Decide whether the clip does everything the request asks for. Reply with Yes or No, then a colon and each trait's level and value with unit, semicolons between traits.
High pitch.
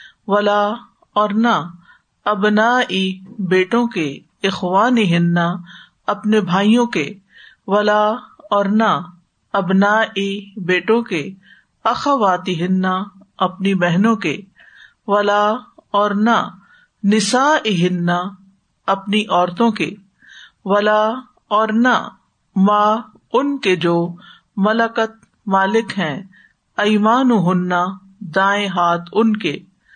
Yes: high, 205 Hz